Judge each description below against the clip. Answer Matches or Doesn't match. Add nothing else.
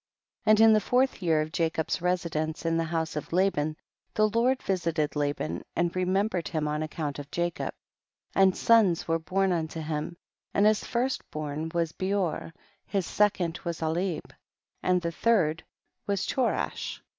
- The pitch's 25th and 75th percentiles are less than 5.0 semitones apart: Matches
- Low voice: Doesn't match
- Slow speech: Doesn't match